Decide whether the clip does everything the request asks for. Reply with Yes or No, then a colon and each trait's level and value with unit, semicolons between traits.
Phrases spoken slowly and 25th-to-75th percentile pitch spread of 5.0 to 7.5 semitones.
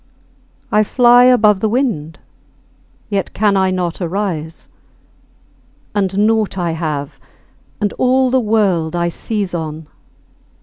No: slow, 120 wpm; average, 4.4 semitones